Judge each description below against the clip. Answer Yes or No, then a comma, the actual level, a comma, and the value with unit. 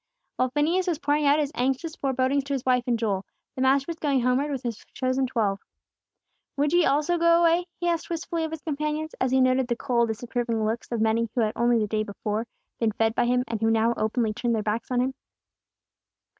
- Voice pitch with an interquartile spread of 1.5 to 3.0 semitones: No, average, 4.3 semitones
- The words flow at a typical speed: No, fast, 225 wpm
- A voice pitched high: Yes, very high, 255 Hz